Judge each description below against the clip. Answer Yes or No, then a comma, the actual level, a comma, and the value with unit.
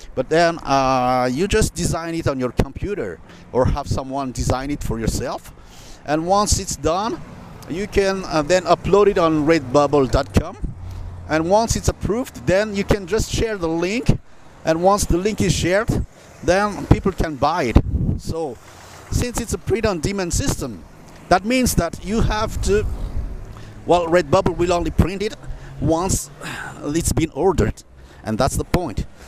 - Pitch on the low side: No, medium, 160 Hz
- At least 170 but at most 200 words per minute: No, average, 160 wpm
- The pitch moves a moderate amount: No, wide, 6.5 semitones